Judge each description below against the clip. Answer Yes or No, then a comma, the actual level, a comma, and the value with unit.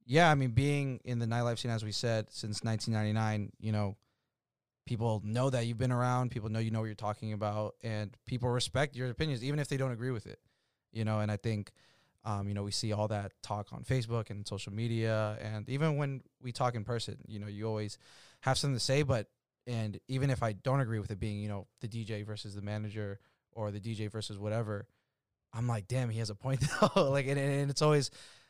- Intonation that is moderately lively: Yes, average, 3.5 semitones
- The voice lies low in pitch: Yes, low, 115 Hz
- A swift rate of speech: Yes, fast, 230 wpm